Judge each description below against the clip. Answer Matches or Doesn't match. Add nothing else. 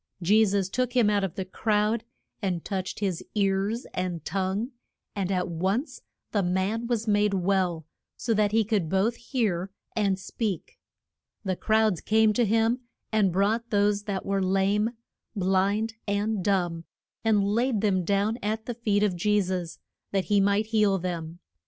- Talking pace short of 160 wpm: Doesn't match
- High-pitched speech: Matches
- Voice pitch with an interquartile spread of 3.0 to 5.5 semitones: Doesn't match